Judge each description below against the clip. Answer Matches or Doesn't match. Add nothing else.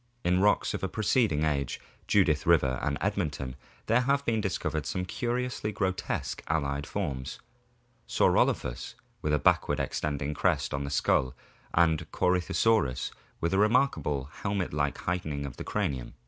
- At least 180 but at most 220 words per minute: Doesn't match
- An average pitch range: Doesn't match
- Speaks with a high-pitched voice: Doesn't match